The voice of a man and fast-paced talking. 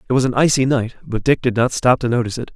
Yes: male; fast, 305 wpm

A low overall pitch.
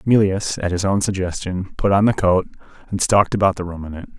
Yes: very low, 95 Hz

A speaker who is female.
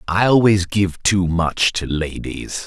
No: male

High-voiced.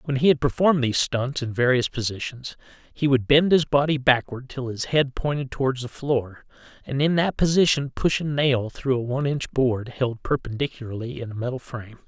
No: low, 130 Hz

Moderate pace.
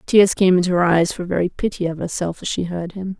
No: fast, 265 wpm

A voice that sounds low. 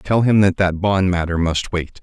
Yes: very low, 95 Hz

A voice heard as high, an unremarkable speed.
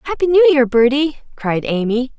Yes: very high, 270 Hz; average, 165 wpm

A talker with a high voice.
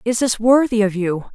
Yes: high, 225 Hz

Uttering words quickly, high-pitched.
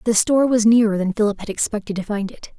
Yes: fast, 255 wpm; high, 215 Hz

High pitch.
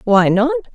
Yes: high, 215 Hz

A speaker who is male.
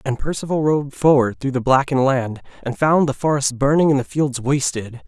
Yes: male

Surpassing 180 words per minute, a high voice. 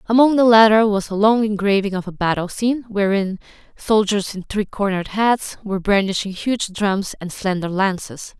No: average, 170 wpm; high, 205 Hz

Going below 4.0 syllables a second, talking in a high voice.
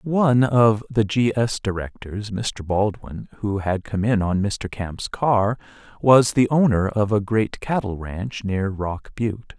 No: 3.8 syllables/s; low, 110 Hz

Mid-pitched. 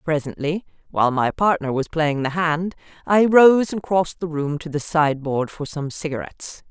Yes: medium, 160 Hz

